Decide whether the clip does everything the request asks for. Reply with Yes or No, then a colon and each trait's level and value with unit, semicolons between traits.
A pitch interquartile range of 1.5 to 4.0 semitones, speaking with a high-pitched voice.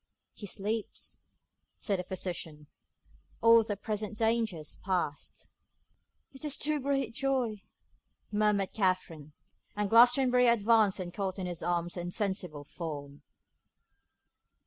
No: average, 4.6 semitones; high, 200 Hz